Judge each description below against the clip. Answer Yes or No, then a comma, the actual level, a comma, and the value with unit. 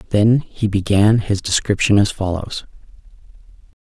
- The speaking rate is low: Yes, slow, 105 wpm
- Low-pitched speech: Yes, low, 105 Hz